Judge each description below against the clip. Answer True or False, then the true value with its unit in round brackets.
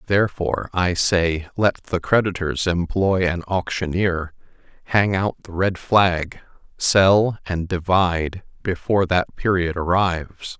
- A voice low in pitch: True (90 Hz)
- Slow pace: True (120 wpm)